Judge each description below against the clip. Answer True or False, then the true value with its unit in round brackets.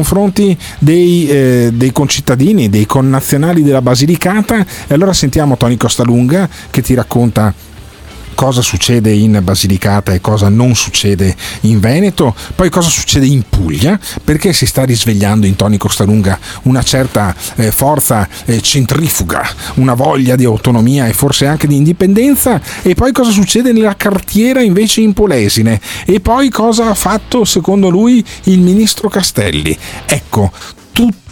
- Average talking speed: True (140 wpm)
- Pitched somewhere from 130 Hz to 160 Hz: True (135 Hz)